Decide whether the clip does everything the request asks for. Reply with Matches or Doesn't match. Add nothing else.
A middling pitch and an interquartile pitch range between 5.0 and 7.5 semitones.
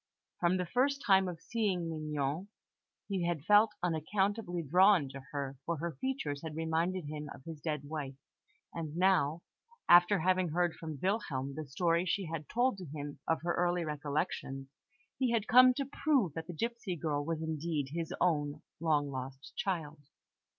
Doesn't match